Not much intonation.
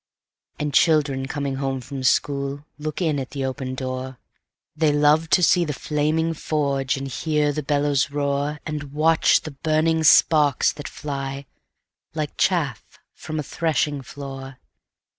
Yes: narrow, 2.1 semitones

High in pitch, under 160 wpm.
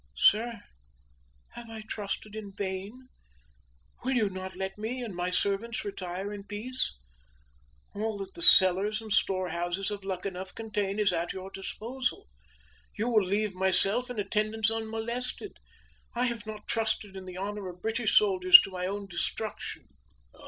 Yes: high, 210 Hz; average, 150 wpm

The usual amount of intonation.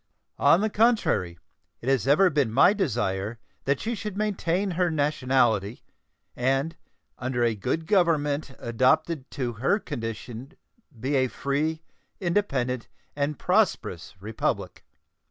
No: wide, 5.9 semitones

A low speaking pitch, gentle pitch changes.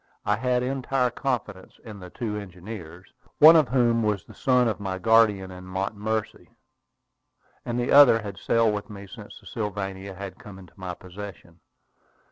No: low, 105 Hz; average, 3.8 semitones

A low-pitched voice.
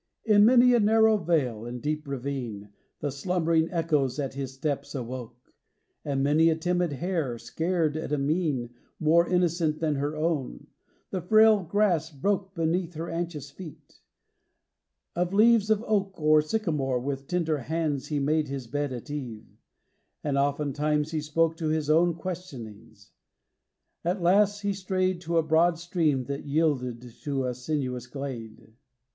No: medium, 155 Hz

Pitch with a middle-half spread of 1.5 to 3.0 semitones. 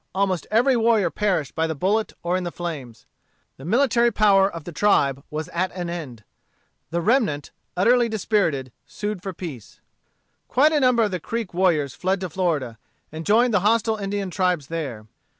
No: average, 5.1 semitones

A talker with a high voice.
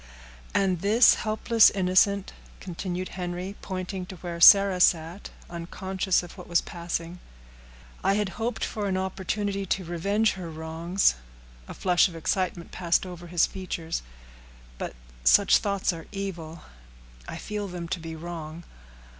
No: medium, 180 Hz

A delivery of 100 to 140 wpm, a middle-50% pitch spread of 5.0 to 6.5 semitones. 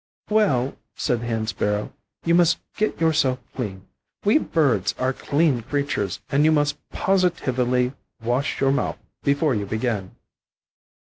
Yes: slow, 135 wpm; wide, 5.4 semitones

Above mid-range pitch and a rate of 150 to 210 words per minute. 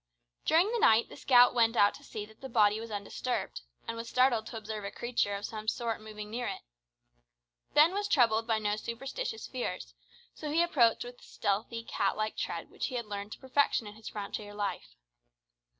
Yes: high, 230 Hz; average, 200 wpm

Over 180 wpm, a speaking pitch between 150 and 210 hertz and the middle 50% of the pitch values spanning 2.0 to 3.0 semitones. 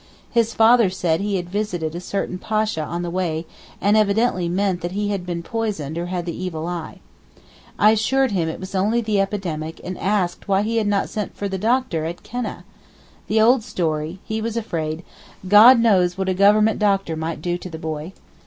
No: average, 200 wpm; high, 190 Hz; average, 3.8 semitones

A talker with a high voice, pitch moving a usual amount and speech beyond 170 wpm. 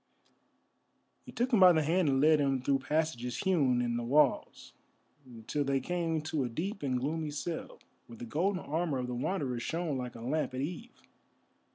No: medium, 145 Hz; average, 4.4 semitones; average, 190 wpm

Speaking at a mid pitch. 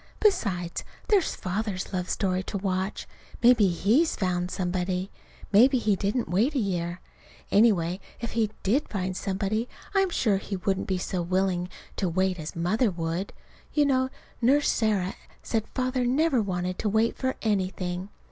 No: high, 195 Hz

